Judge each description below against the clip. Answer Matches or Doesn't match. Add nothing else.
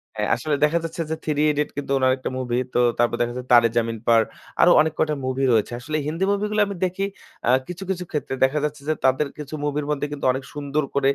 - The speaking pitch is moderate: Matches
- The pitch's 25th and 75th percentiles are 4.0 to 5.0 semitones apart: Doesn't match